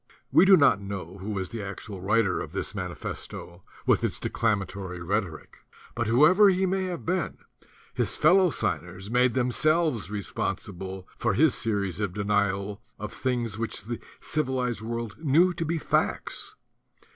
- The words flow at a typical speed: Yes, average, 150 wpm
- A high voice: No, low, 115 Hz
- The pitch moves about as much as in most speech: No, wide, 7.4 semitones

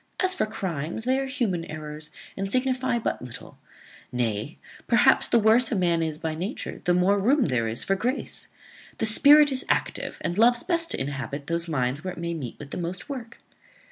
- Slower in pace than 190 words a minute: No, average, 200 wpm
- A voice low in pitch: No, medium, 185 Hz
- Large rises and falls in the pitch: Yes, wide, 8.0 semitones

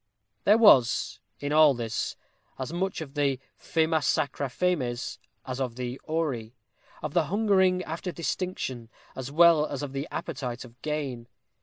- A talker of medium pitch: Yes, medium, 145 Hz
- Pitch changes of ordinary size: Yes, average, 4.8 semitones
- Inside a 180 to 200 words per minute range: No, average, 150 wpm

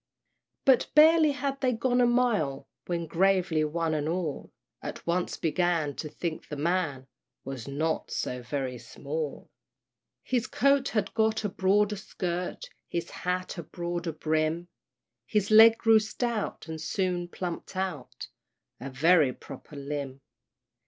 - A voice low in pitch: No, medium, 175 Hz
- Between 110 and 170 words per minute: Yes, average, 140 wpm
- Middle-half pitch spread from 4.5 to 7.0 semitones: Yes, wide, 5.6 semitones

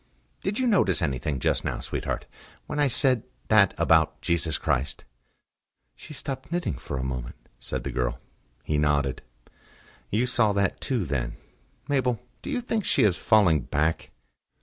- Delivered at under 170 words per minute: Yes, average, 155 wpm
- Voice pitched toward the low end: Yes, very low, 90 Hz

